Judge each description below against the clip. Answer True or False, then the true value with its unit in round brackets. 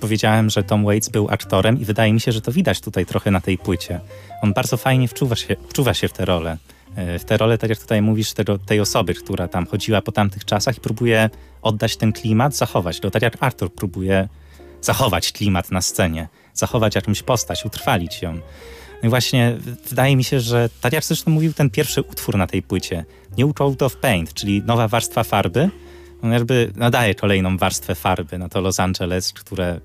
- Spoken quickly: True (205 wpm)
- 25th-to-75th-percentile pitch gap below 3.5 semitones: False (4.1 semitones)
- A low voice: True (105 Hz)